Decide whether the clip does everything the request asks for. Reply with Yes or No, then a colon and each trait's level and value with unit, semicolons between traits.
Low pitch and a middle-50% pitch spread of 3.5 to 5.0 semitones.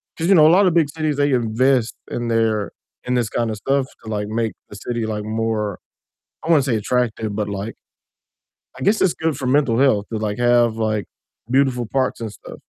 Yes: low, 120 Hz; average, 4.0 semitones